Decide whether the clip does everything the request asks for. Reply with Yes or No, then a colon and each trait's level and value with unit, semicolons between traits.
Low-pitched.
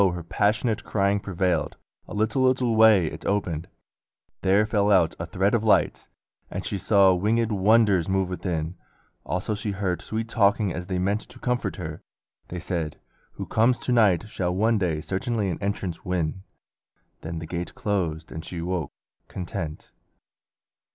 Yes: very low, 95 Hz